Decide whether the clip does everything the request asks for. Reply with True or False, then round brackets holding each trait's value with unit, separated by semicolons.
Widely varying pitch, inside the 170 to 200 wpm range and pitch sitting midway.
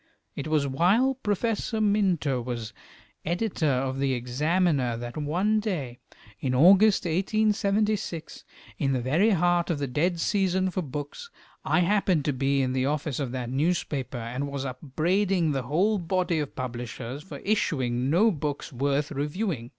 False (6.1 semitones; 155 wpm; 150 Hz)